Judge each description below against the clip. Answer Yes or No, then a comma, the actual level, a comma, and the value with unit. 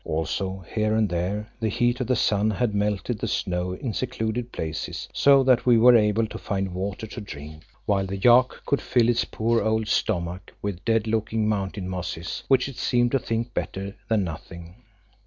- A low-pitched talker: Yes, low, 105 Hz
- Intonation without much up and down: No, average, 3.7 semitones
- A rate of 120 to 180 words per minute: No, average, 190 wpm